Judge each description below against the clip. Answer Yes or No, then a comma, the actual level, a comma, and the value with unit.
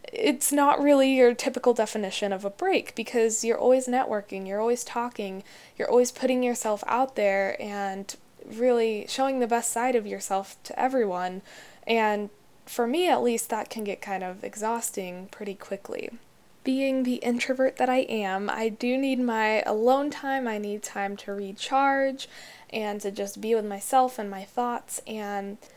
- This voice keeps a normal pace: Yes, average, 170 wpm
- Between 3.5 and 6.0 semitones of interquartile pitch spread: Yes, average, 4.2 semitones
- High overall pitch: Yes, high, 230 Hz